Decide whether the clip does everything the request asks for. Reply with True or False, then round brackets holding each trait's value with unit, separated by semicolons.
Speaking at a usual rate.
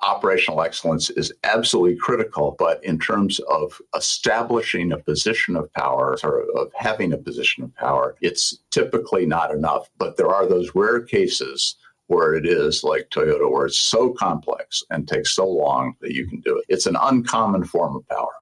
True (180 wpm)